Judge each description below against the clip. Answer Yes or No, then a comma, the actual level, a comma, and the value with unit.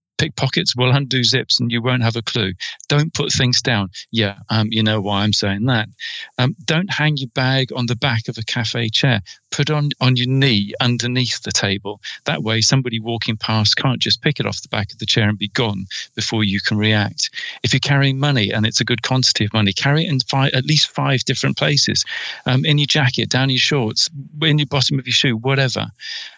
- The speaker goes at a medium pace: No, fast, 225 wpm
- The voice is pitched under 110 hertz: No, low, 125 Hz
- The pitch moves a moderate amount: Yes, average, 3.8 semitones